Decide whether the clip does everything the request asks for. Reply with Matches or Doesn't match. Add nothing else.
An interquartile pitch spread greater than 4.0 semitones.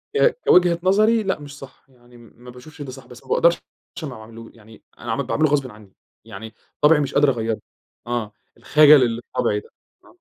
Matches